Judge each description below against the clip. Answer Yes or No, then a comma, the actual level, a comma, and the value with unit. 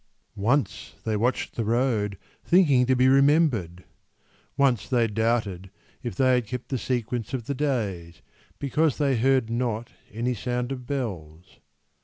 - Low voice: Yes, low, 120 Hz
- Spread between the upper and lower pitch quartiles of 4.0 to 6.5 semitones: No, average, 3.5 semitones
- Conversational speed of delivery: Yes, average, 145 wpm